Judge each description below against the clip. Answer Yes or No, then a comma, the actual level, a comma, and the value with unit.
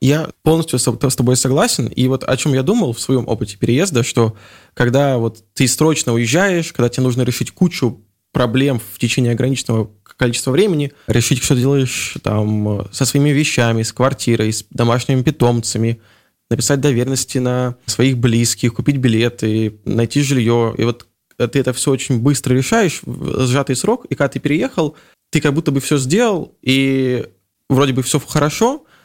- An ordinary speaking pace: No, fast, 165 wpm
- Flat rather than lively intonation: No, average, 3.3 semitones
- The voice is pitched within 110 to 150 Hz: Yes, low, 130 Hz